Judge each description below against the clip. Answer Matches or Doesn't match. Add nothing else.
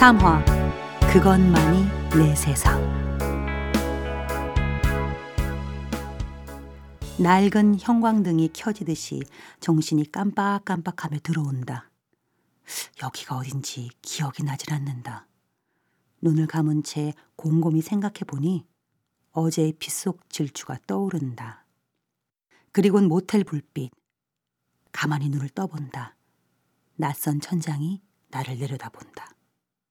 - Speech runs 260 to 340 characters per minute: Doesn't match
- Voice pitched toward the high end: Doesn't match